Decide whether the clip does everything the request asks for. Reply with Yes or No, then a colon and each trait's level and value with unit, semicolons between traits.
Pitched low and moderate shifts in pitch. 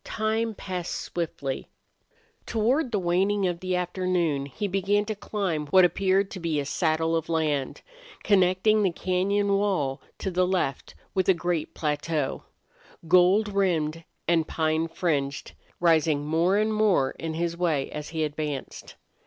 No: medium, 175 Hz; average, 3.8 semitones